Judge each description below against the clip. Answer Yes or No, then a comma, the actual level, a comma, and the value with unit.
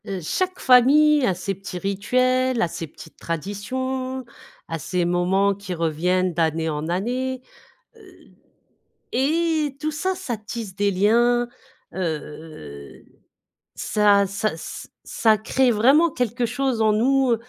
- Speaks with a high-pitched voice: Yes, high, 215 Hz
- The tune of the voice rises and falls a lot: Yes, wide, 6.2 semitones